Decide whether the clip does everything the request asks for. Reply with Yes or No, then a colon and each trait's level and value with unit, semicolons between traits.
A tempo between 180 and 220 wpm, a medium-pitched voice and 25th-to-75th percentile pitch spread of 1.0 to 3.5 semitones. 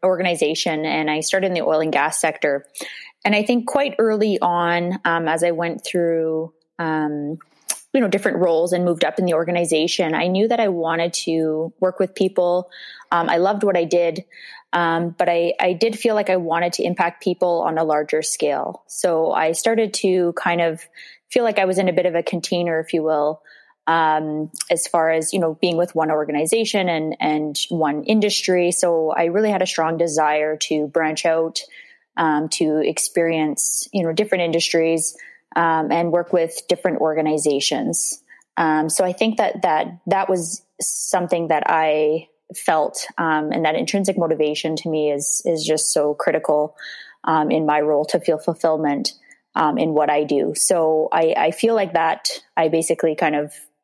Yes: average, 185 wpm; medium, 165 Hz; narrow, 2.6 semitones